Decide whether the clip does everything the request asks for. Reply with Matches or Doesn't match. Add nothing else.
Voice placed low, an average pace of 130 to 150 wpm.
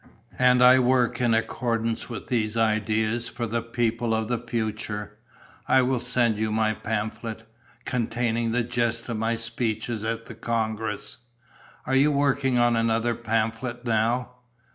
Matches